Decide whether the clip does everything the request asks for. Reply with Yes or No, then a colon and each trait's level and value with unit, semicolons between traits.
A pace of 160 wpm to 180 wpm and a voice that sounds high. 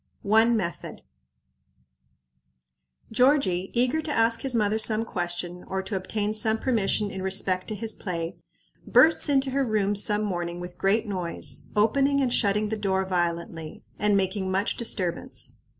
No: average, 150 wpm; high, 205 Hz